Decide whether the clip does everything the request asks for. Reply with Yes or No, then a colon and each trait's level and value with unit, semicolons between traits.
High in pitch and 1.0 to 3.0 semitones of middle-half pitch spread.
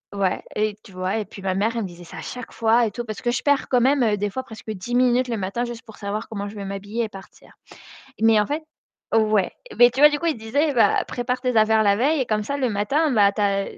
No: high, 220 Hz; average, 3.5 semitones